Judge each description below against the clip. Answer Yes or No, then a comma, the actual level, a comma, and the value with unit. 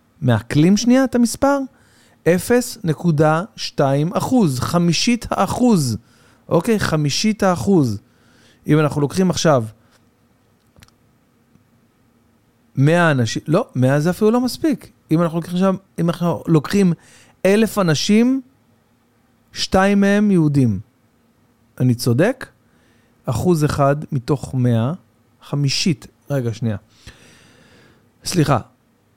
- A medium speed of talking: No, slow, 85 wpm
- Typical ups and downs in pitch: No, wide, 7.3 semitones